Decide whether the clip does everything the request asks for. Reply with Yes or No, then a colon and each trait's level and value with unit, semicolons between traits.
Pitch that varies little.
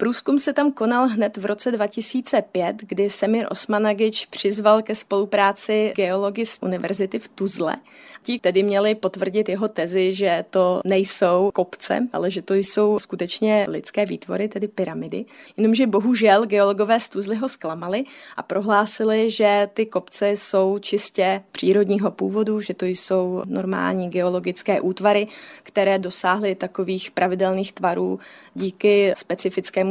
Yes: narrow, 2.2 semitones